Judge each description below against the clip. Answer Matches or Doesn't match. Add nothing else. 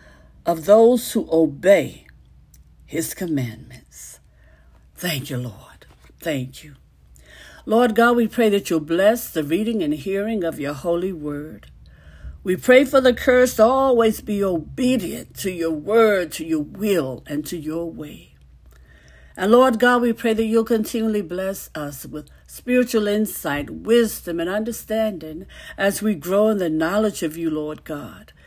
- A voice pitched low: Doesn't match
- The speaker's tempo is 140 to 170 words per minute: Matches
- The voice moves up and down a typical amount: Doesn't match